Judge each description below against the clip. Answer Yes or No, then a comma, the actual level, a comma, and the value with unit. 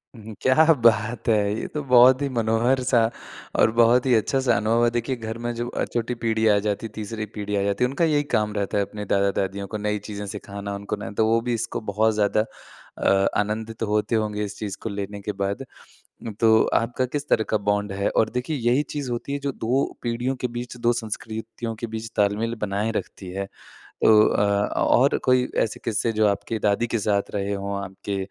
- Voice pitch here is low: Yes, low, 110 Hz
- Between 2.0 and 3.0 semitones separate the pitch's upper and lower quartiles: Yes, average, 2.7 semitones